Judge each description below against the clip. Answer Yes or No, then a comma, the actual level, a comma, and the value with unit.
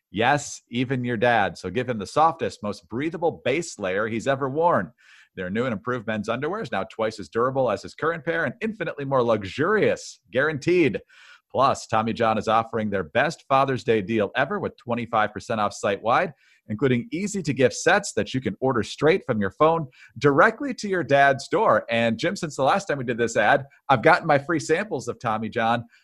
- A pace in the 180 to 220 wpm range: Yes, average, 200 wpm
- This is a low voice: Yes, low, 130 Hz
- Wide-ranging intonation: Yes, wide, 5.8 semitones